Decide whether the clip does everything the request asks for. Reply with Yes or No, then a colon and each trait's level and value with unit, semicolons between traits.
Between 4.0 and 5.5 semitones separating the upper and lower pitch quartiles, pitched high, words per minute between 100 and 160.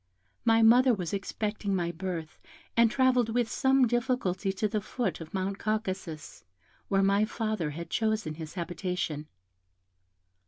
Yes: average, 4.3 semitones; high, 200 Hz; average, 140 wpm